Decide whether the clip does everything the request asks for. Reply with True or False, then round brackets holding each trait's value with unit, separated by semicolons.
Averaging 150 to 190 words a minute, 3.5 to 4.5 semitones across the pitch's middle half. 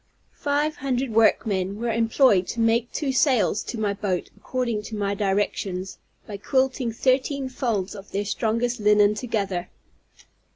False (140 wpm; 4.0 semitones)